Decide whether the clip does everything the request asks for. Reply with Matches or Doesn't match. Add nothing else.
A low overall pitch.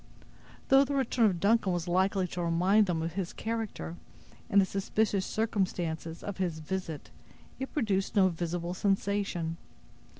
Doesn't match